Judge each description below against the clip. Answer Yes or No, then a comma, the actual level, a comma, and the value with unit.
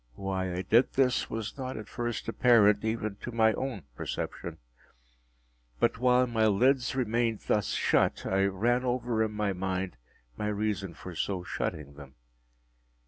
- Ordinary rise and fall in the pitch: Yes, average, 3.8 semitones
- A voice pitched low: Yes, low, 110 Hz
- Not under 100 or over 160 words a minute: Yes, average, 150 wpm